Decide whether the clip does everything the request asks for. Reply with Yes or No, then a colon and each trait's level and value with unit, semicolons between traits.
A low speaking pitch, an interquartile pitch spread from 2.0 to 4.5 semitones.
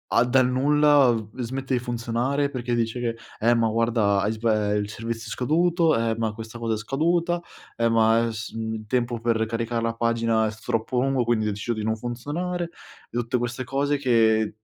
Yes: low, 115 Hz; narrow, 2.5 semitones